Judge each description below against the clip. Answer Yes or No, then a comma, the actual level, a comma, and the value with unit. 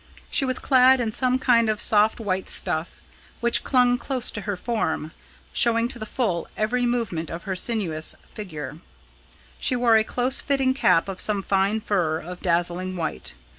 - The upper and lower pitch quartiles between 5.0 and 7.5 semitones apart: Yes, average, 5.3 semitones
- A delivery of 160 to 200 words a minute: Yes, average, 170 wpm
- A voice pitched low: No, high, 215 Hz